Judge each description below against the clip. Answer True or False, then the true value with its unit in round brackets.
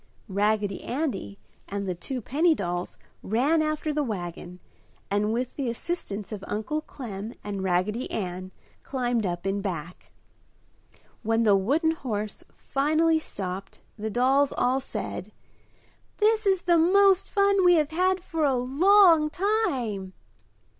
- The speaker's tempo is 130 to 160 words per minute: True (135 wpm)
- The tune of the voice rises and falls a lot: True (8.2 semitones)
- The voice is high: True (245 Hz)